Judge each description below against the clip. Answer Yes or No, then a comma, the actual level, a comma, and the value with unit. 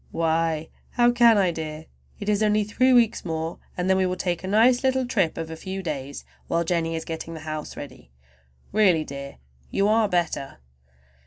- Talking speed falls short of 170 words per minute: No, average, 190 wpm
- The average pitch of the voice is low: No, medium, 180 Hz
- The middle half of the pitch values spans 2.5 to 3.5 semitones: No, average, 4.7 semitones